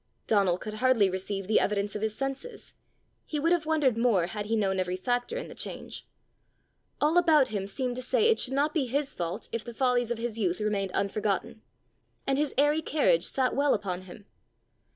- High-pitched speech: Yes, high, 235 Hz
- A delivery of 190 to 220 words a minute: Yes, average, 200 wpm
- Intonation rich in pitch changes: Yes, wide, 5.7 semitones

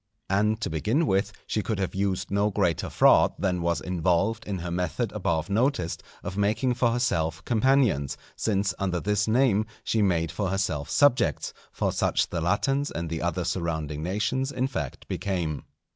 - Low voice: Yes, very low, 95 Hz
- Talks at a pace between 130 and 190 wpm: Yes, average, 170 wpm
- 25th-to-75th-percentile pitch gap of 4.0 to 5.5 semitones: Yes, average, 4.4 semitones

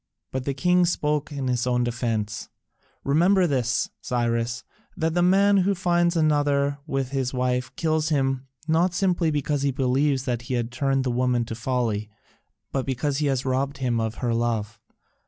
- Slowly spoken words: No, average, 175 wpm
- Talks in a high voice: No, low, 135 Hz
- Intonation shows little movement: No, average, 3.9 semitones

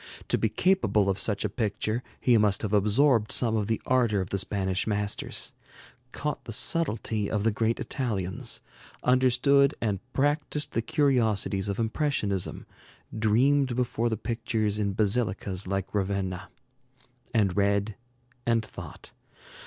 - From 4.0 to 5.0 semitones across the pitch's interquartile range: No, average, 3.6 semitones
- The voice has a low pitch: Yes, low, 110 Hz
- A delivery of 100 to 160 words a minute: Yes, slow, 135 wpm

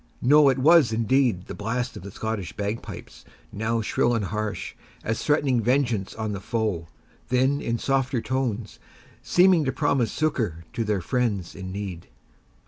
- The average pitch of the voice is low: Yes, low, 115 Hz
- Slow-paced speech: No, average, 155 wpm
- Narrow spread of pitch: No, average, 4.3 semitones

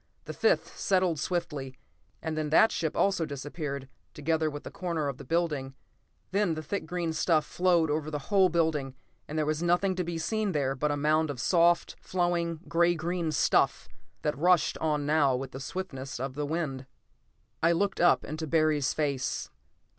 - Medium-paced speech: Yes, average, 180 wpm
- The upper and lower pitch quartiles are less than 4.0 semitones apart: Yes, average, 2.9 semitones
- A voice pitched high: No, medium, 155 Hz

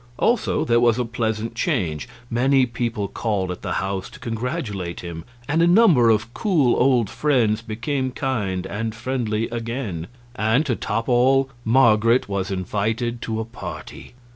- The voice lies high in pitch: No, low, 115 Hz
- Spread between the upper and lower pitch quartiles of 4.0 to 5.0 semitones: No, average, 3.3 semitones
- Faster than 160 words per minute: No, average, 155 wpm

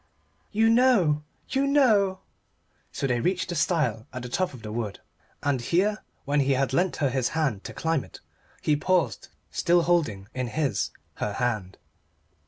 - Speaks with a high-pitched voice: No, medium, 150 Hz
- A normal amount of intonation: No, wide, 6.9 semitones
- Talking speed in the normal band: Yes, average, 170 wpm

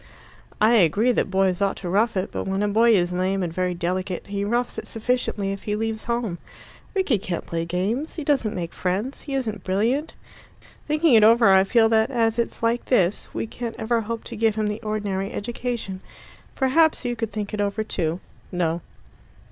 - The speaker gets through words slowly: No, average, 195 wpm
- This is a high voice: Yes, high, 215 Hz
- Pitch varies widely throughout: No, average, 3.6 semitones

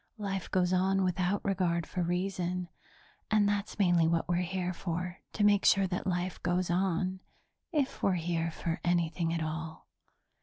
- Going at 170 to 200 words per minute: No, average, 160 wpm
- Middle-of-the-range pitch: Yes, medium, 180 Hz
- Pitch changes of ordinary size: No, narrow, 2.0 semitones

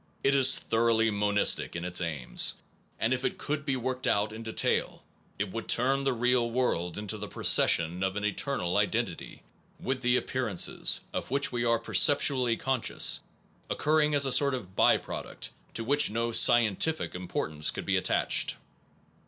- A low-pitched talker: Yes, low, 115 Hz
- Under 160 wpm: No, average, 170 wpm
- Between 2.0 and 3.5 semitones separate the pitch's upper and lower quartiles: No, average, 4.3 semitones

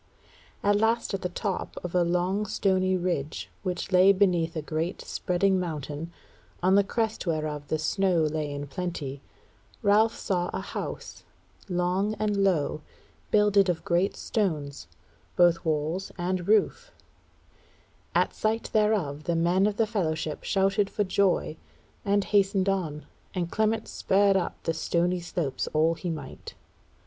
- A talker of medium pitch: Yes, medium, 180 Hz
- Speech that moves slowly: No, average, 145 wpm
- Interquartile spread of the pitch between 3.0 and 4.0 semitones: Yes, average, 3.6 semitones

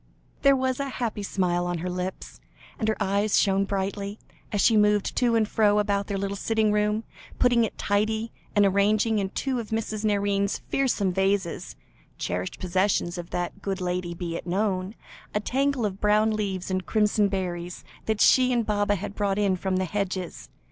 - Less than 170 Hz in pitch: No, high, 205 Hz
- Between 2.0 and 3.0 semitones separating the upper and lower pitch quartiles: Yes, narrow, 2.4 semitones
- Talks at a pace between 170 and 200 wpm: Yes, average, 180 wpm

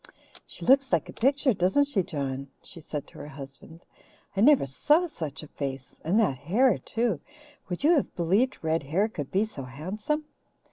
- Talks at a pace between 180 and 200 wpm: Yes, average, 185 wpm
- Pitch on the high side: No, medium, 180 Hz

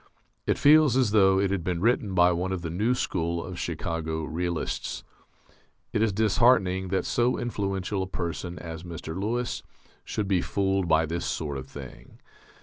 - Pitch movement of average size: Yes, average, 3.7 semitones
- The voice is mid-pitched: No, very low, 95 Hz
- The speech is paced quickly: No, average, 170 wpm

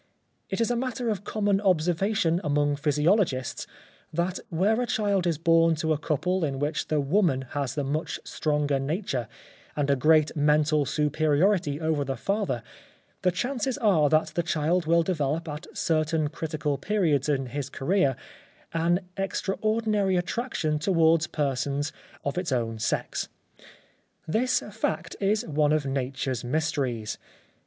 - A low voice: No, medium, 155 Hz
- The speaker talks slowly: No, average, 145 wpm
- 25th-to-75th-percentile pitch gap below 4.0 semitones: No, average, 4.5 semitones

